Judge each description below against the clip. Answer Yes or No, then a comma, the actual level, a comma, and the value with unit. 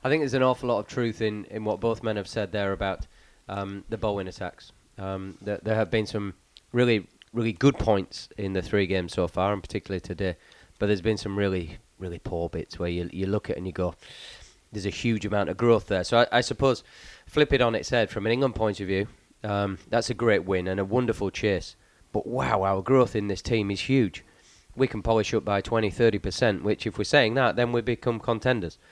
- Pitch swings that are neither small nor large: Yes, average, 3.2 semitones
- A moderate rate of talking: No, fast, 235 wpm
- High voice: No, low, 105 Hz